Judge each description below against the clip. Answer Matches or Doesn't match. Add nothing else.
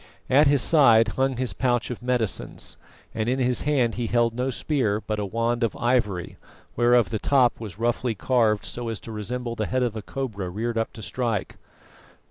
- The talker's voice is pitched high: Doesn't match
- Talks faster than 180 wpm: Matches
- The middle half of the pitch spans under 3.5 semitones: Matches